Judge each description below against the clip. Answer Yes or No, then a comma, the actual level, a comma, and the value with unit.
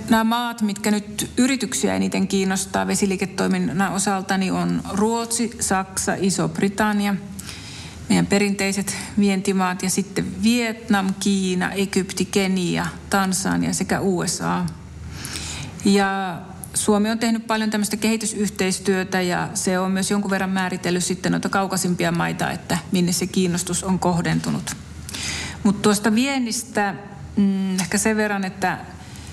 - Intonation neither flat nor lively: No, narrow, 2.3 semitones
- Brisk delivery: No, average, 120 wpm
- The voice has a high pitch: Yes, high, 195 Hz